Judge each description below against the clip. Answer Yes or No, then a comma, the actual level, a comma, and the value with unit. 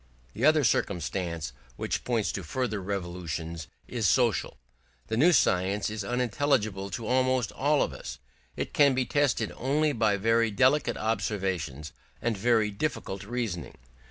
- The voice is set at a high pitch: No, low, 110 Hz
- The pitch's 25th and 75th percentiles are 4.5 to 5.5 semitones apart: Yes, average, 5.1 semitones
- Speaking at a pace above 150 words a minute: No, average, 140 wpm